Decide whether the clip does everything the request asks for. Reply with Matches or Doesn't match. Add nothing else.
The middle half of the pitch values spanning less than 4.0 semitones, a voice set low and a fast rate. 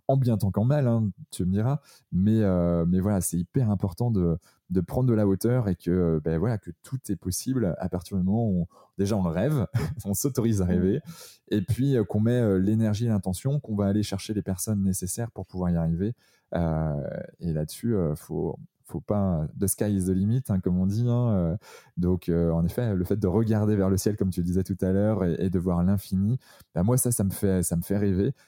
Matches